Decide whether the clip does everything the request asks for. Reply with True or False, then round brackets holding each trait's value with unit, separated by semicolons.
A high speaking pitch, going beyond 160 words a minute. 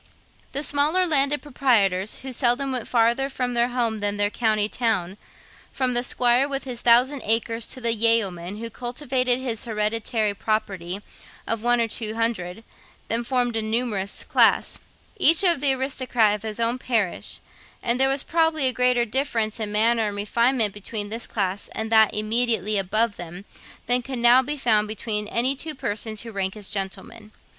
True (230 Hz; 170 wpm)